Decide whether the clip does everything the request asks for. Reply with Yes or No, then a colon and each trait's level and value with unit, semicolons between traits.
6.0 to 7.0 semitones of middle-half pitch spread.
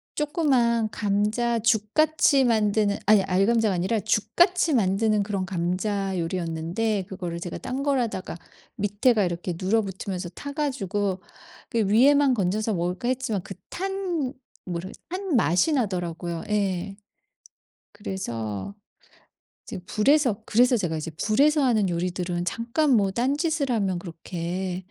No: average, 5.2 semitones